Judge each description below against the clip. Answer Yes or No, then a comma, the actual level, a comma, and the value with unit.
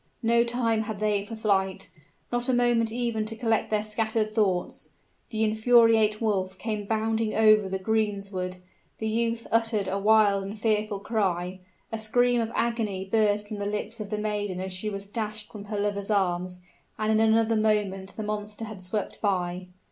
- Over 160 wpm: Yes, average, 180 wpm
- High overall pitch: Yes, high, 215 Hz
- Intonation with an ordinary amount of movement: No, narrow, 1.9 semitones